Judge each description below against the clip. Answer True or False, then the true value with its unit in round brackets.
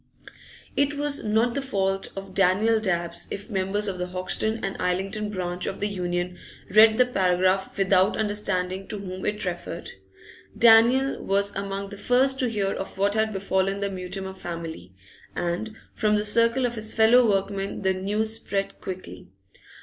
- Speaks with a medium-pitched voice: False (195 Hz)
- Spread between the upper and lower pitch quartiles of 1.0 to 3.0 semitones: True (2.7 semitones)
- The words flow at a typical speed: True (165 wpm)